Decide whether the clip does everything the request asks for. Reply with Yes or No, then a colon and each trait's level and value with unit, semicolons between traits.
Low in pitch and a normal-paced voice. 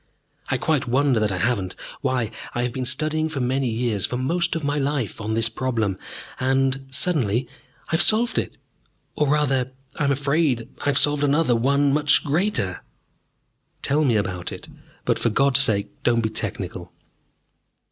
Yes: low, 130 Hz; average, 170 wpm